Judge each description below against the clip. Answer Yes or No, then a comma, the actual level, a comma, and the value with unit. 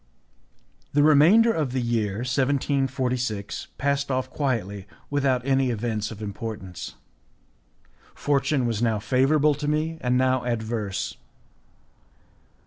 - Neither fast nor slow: No, slow, 110 wpm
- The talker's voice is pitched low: Yes, low, 130 Hz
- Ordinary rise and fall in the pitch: Yes, average, 4.0 semitones